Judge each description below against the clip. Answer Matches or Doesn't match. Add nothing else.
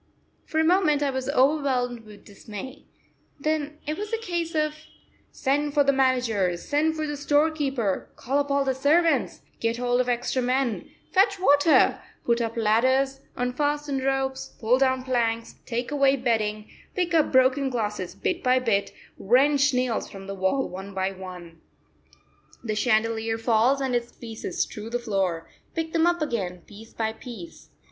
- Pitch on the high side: Matches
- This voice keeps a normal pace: Matches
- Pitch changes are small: Doesn't match